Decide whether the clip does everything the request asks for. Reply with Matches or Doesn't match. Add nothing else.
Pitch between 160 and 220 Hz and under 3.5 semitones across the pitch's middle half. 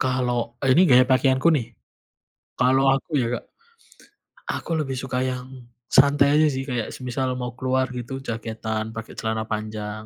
Doesn't match